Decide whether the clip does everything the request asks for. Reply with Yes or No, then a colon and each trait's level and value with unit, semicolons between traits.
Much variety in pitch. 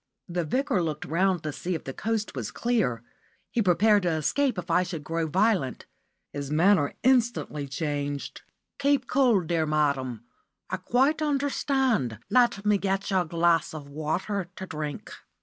Yes: wide, 6.7 semitones